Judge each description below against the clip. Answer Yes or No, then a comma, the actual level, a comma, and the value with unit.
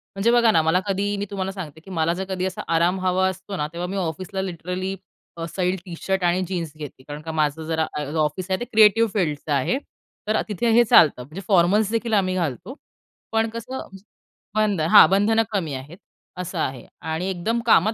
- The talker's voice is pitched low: No, medium, 185 Hz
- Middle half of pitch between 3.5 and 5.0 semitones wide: Yes, average, 4.0 semitones